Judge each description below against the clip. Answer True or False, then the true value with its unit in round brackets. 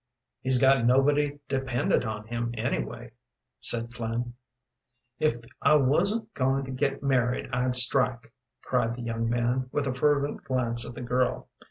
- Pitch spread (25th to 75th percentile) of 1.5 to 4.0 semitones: True (2.4 semitones)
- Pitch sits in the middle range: False (125 Hz)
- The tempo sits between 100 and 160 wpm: True (150 wpm)